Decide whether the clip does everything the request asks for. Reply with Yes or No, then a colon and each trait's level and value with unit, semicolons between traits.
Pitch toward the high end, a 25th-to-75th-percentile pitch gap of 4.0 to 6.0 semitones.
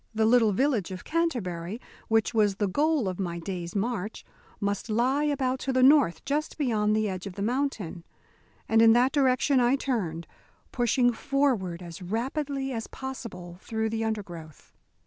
Yes: high, 225 Hz; wide, 5.6 semitones